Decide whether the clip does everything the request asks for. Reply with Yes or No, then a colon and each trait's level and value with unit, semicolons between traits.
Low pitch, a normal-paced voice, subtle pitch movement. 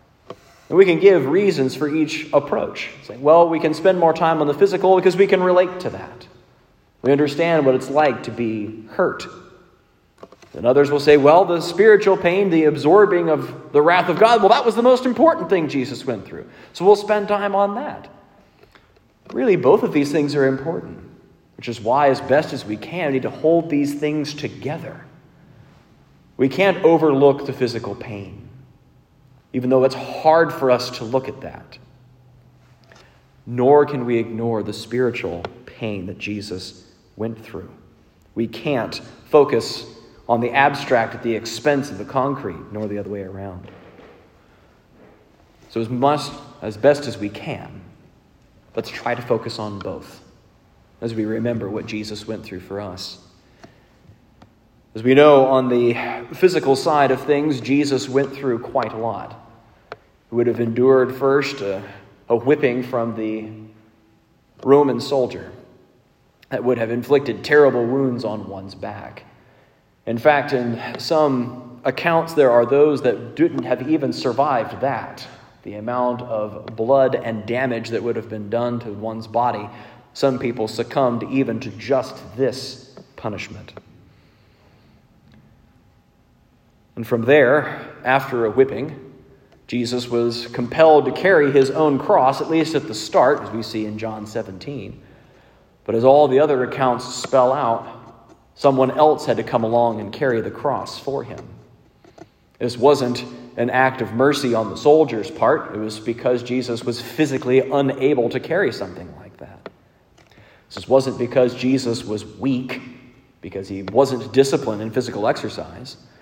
No: low, 130 Hz; average, 155 wpm; average, 4.1 semitones